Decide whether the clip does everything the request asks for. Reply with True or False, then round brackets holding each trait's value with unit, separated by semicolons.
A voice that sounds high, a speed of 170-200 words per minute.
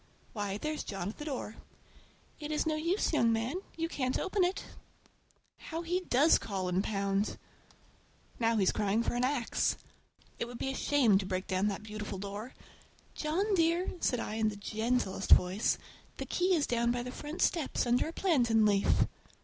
True (240 Hz; 180 wpm)